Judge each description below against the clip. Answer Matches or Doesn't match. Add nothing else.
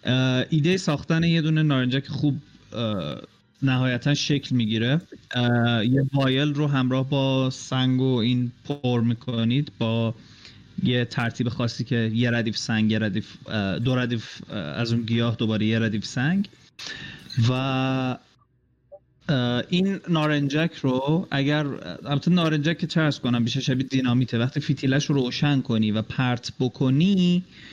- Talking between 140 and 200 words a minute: Doesn't match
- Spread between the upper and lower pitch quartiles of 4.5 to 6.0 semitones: Doesn't match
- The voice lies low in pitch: Matches